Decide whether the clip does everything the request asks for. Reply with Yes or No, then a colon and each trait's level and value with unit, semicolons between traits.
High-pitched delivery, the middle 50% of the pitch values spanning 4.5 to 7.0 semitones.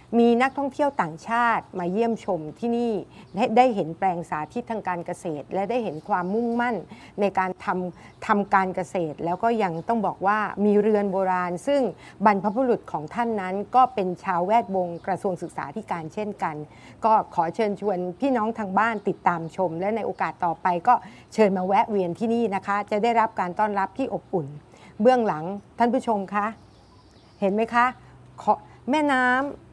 No: high, 205 Hz; average, 4.1 semitones